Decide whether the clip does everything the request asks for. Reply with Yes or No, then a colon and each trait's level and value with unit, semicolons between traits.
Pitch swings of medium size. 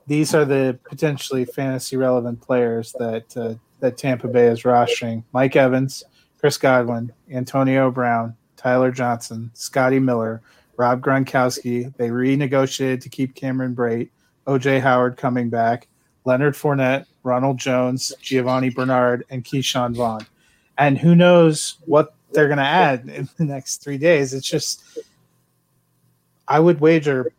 No: narrow, 2.2 semitones